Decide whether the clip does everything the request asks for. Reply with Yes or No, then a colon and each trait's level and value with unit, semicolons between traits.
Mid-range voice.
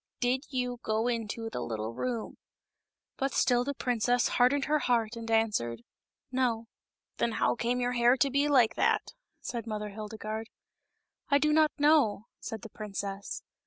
No: high, 235 Hz